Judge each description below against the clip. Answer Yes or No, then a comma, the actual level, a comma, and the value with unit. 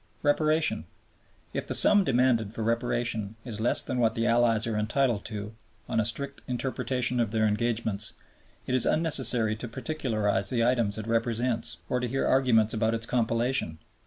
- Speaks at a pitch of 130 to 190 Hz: No, low, 115 Hz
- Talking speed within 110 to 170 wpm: Yes, average, 165 wpm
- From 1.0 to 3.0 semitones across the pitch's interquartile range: Yes, narrow, 2.5 semitones